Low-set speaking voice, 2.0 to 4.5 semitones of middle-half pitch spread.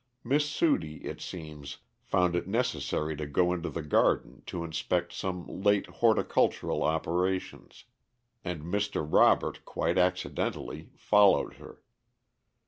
Yes: very low, 90 Hz; average, 4.2 semitones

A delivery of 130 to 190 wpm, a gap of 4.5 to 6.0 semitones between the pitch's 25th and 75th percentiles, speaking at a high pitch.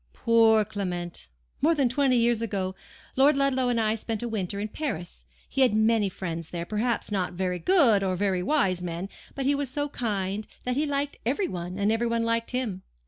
No: average, 200 wpm; average, 5.2 semitones; high, 225 Hz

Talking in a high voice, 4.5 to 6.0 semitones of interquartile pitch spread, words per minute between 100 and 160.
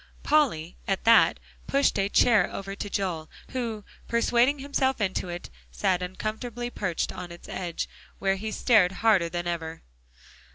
Yes: high, 200 Hz; average, 5.0 semitones; average, 150 wpm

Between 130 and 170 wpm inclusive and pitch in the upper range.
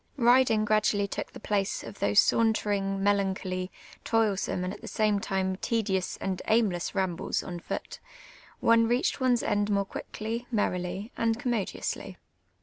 Yes: average, 145 wpm; high, 205 Hz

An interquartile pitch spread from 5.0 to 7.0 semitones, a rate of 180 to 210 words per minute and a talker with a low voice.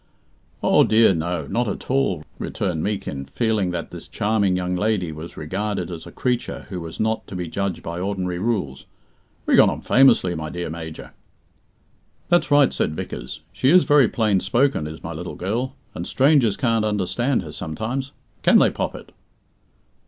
No: wide, 5.4 semitones; average, 170 wpm; low, 100 Hz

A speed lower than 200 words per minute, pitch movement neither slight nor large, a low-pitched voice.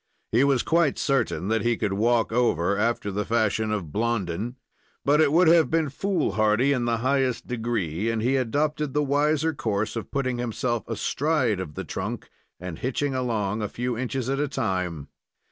Yes: average, 180 wpm; average, 4.5 semitones; low, 120 Hz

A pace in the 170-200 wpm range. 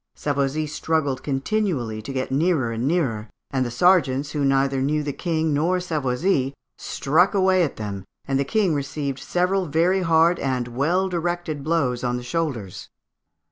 No: average, 160 wpm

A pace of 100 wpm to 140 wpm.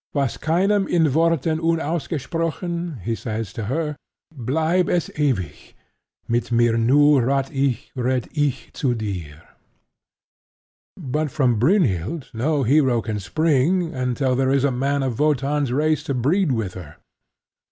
Yes: slow, 135 wpm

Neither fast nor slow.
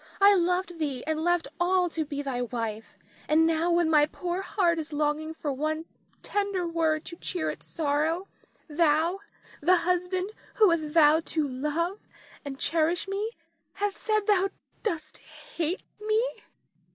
Yes: average, 150 wpm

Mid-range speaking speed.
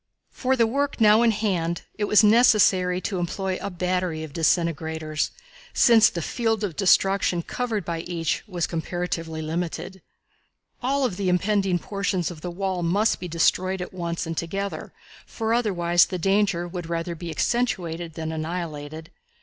Yes: average, 160 wpm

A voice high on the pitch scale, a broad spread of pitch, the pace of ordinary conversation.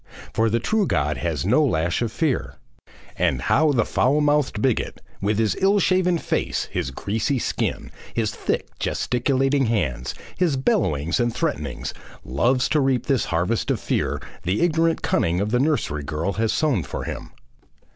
No: low, 120 Hz; wide, 8.4 semitones; average, 165 wpm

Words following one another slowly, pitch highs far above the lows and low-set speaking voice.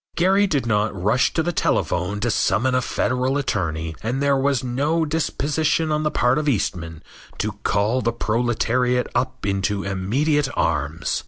No: average, 160 wpm; wide, 5.9 semitones; low, 125 Hz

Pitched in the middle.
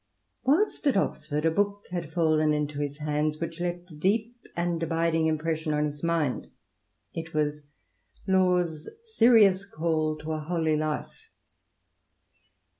Yes: medium, 160 Hz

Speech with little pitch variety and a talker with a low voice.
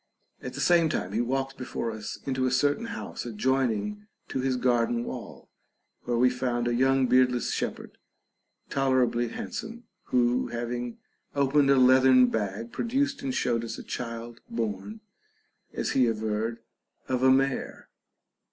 Yes: narrow, 2.3 semitones; low, 125 Hz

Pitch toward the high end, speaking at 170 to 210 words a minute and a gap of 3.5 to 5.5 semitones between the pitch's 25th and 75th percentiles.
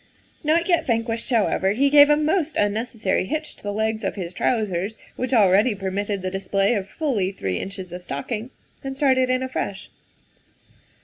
Yes: high, 220 Hz; average, 175 wpm; average, 5.1 semitones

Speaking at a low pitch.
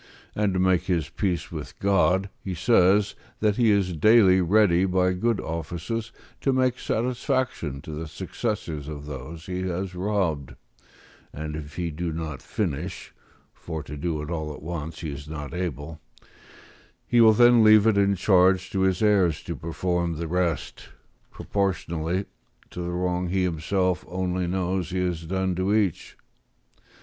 Yes: very low, 90 Hz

